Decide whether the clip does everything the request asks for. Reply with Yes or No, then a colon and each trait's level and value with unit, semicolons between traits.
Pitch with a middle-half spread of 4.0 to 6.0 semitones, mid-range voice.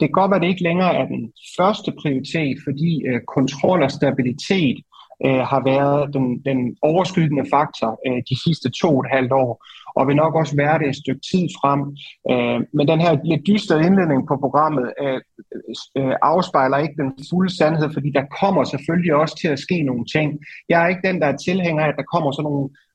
No: average, 3.6 semitones; medium, 145 Hz